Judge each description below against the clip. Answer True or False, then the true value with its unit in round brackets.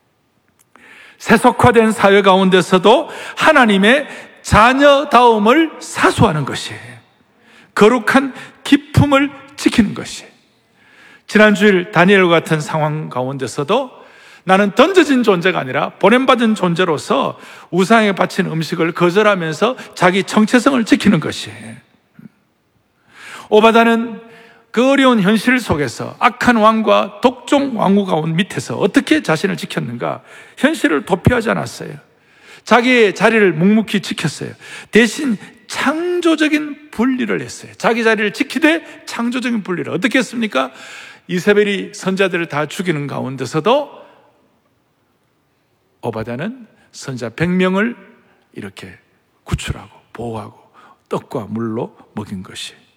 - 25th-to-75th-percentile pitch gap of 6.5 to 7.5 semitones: False (5.4 semitones)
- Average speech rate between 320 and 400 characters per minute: False (265 characters per minute)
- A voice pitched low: False (215 Hz)